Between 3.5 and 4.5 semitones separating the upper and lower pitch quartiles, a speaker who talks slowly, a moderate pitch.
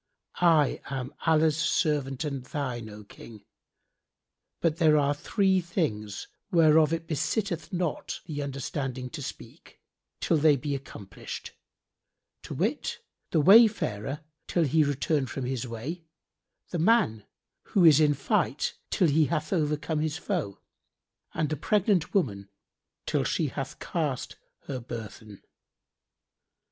Yes: average, 4.0 semitones; slow, 130 wpm; medium, 150 Hz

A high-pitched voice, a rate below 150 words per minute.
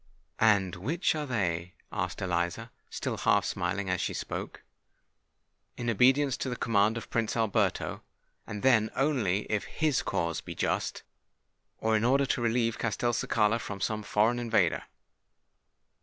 No: low, 110 Hz; average, 140 wpm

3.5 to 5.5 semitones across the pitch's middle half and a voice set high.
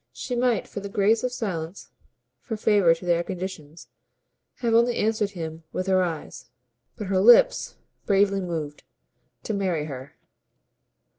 Yes: average, 4.6 semitones; high, 195 Hz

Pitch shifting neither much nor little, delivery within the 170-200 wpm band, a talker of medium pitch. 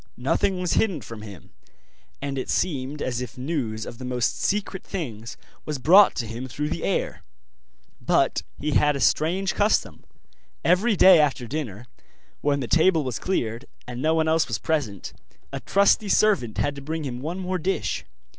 No: wide, 6.4 semitones; average, 175 wpm; medium, 145 Hz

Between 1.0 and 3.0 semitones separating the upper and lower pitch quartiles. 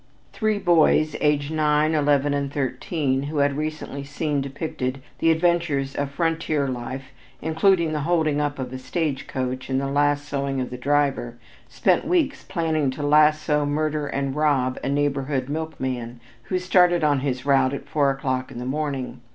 Yes: narrow, 2.4 semitones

